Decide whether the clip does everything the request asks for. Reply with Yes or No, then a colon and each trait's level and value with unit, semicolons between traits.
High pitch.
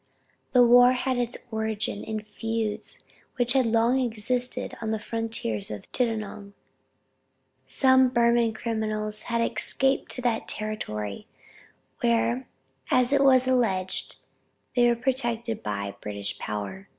Yes: high, 225 Hz